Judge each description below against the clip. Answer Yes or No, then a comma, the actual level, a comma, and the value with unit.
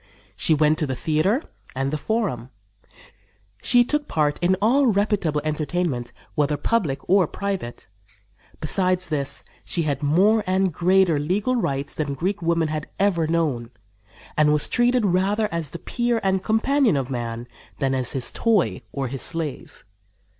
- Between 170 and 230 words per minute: No, average, 155 wpm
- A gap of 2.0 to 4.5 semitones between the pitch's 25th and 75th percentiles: No, wide, 5.6 semitones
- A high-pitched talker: No, medium, 165 Hz